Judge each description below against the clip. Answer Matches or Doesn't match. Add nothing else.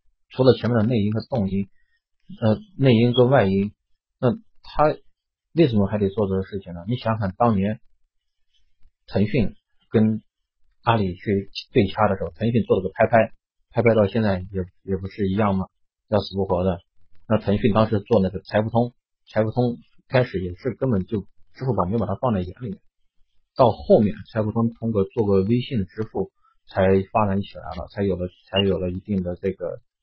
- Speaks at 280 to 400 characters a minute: Doesn't match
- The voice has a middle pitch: Doesn't match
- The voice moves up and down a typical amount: Matches